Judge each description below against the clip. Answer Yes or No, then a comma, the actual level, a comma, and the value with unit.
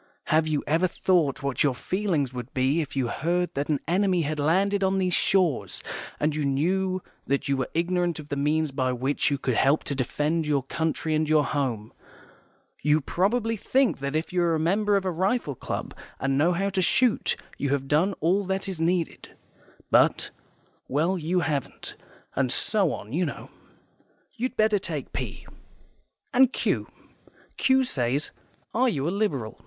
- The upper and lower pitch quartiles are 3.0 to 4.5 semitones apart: No, average, 5.1 semitones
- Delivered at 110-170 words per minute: No, average, 180 wpm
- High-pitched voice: No, medium, 160 Hz